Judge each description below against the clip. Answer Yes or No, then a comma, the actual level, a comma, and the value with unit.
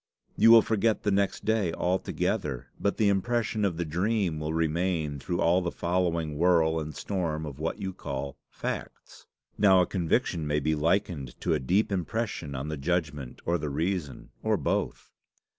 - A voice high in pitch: No, very low, 85 Hz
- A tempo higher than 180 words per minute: No, average, 175 wpm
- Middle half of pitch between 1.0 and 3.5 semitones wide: No, average, 4.2 semitones